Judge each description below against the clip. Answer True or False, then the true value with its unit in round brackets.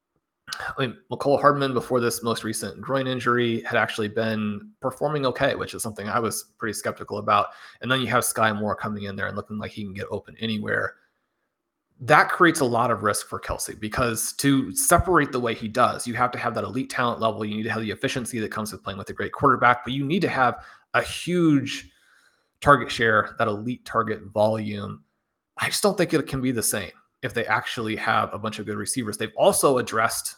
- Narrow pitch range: False (3.3 semitones)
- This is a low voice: True (115 Hz)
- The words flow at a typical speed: False (220 wpm)